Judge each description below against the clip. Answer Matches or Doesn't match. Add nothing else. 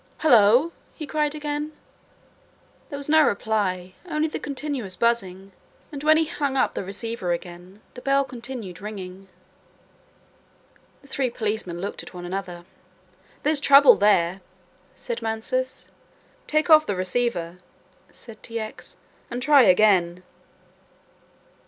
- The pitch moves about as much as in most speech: Doesn't match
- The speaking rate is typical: Doesn't match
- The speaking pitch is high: Matches